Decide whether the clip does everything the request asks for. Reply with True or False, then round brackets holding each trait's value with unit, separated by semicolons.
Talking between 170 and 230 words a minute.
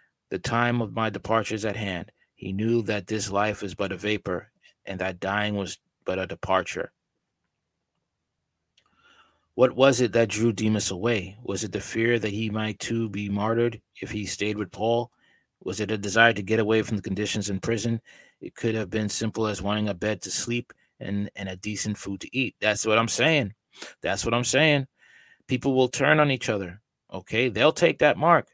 True (200 wpm)